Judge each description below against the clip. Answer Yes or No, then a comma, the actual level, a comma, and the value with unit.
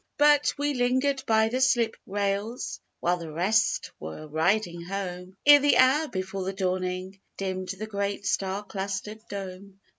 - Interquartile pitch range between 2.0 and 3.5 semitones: No, average, 3.9 semitones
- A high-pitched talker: Yes, high, 200 Hz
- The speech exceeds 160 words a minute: No, average, 150 wpm